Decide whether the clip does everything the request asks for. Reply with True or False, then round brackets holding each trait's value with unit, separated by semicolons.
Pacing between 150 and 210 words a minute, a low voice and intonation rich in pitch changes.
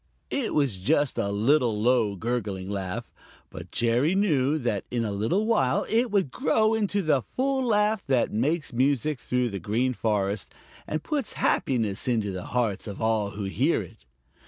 True (170 wpm; 125 Hz; 7.0 semitones)